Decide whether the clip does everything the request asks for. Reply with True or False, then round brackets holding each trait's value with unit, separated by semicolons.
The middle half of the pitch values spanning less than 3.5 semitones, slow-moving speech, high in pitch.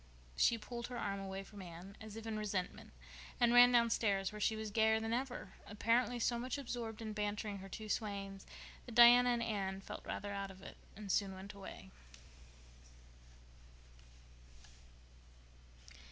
False (3.0 semitones; 155 wpm; 215 Hz)